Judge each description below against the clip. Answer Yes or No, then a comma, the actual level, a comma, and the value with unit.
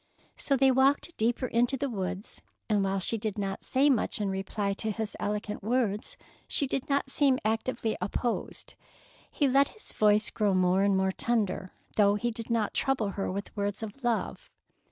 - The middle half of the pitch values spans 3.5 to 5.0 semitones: Yes, average, 4.2 semitones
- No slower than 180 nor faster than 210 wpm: Yes, average, 185 wpm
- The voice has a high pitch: Yes, high, 220 Hz